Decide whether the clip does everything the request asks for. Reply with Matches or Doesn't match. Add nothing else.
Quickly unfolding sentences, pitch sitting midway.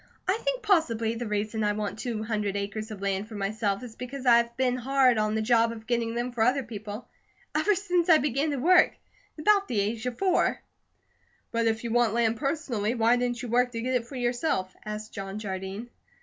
Doesn't match